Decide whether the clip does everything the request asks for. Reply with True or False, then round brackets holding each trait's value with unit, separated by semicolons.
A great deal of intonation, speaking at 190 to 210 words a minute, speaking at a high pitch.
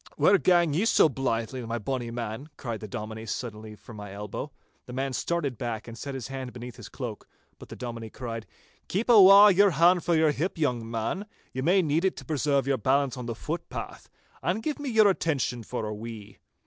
False (6.7 semitones; 200 wpm; 130 Hz)